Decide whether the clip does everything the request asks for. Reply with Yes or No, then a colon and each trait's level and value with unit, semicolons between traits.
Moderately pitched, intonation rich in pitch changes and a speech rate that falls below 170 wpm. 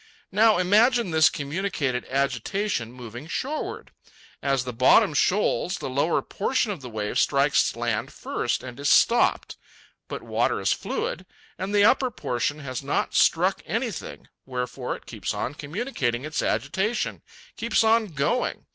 Yes: medium, 150 Hz; wide, 8.6 semitones; average, 145 wpm